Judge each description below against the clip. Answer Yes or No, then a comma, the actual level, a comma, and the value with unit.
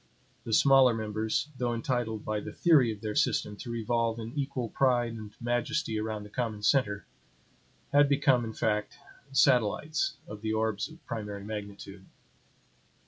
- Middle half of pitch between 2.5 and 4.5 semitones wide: Yes, average, 3.1 semitones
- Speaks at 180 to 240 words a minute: No, average, 150 wpm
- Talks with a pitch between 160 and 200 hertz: No, low, 115 Hz